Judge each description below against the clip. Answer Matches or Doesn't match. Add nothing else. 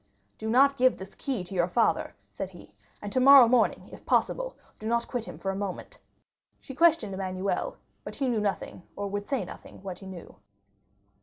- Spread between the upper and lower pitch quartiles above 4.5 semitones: Matches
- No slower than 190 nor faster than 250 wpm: Matches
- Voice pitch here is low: Doesn't match